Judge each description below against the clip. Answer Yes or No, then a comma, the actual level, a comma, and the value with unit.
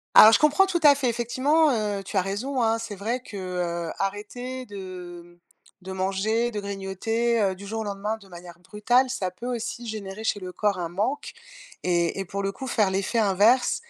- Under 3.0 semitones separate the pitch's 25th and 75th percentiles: No, average, 3.8 semitones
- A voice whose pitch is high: Yes, high, 205 Hz